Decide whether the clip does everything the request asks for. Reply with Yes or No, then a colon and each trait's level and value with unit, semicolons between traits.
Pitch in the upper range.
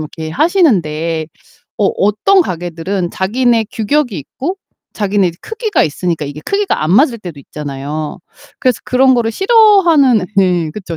Yes: high, 200 Hz